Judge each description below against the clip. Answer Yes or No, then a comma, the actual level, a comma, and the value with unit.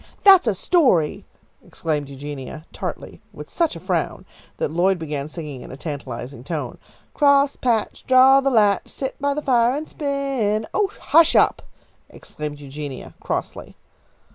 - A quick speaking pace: No, average, 140 wpm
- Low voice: No, high, 200 Hz